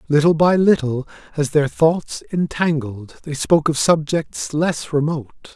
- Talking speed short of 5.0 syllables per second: Yes, 4.5 syllables/s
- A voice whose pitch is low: No, medium, 150 Hz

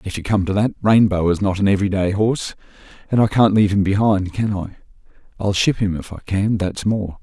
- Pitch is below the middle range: Yes, low, 100 Hz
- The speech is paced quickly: Yes, fast, 235 wpm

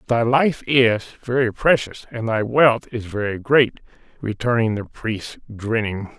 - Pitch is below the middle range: Yes, low, 115 Hz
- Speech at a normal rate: Yes, average, 145 wpm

